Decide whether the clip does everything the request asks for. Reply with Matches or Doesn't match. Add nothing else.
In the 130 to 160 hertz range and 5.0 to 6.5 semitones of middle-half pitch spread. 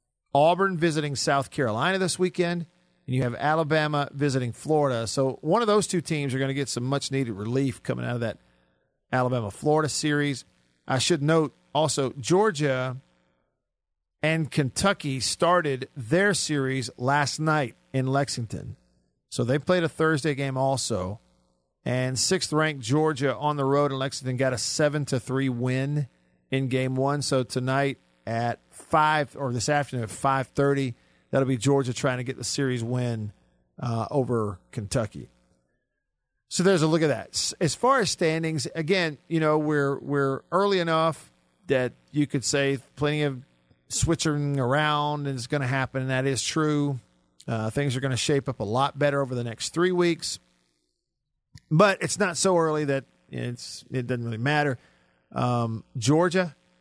Doesn't match